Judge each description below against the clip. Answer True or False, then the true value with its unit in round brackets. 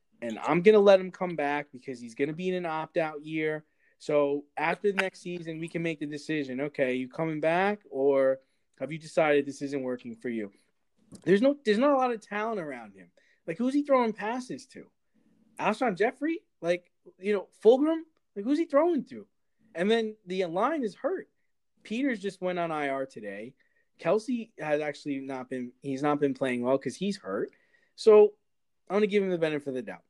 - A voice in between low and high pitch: True (175 Hz)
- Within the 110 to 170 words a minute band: False (200 wpm)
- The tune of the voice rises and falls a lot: True (7.8 semitones)